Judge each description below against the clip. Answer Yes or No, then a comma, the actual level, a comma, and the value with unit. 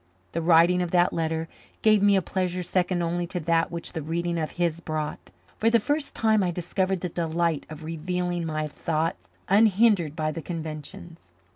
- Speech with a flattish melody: Yes, narrow, 2.1 semitones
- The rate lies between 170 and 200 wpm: Yes, average, 180 wpm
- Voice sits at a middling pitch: Yes, medium, 170 Hz